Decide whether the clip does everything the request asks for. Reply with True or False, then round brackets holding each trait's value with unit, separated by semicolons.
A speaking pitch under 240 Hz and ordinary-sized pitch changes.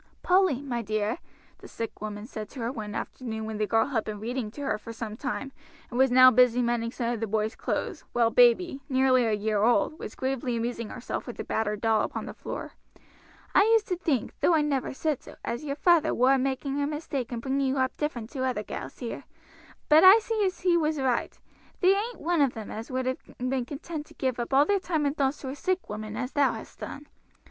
False (255 Hz; 4.2 semitones)